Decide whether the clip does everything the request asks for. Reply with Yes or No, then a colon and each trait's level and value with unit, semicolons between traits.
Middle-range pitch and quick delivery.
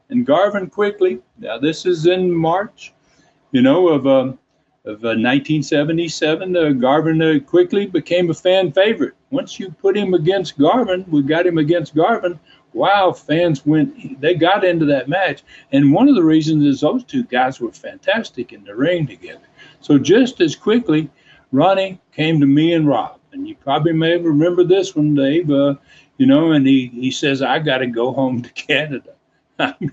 No: medium, 170 Hz; average, 175 wpm